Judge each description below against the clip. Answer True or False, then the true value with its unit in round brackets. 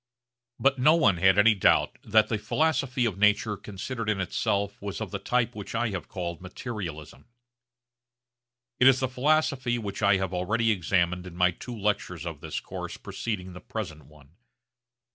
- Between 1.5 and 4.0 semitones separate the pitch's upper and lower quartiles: False (4.6 semitones)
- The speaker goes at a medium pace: True (170 wpm)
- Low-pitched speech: True (105 Hz)